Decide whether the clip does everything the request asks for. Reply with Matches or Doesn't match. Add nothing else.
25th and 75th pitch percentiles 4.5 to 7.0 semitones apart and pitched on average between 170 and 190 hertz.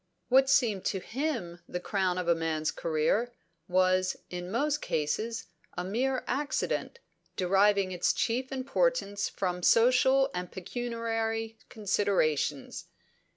Doesn't match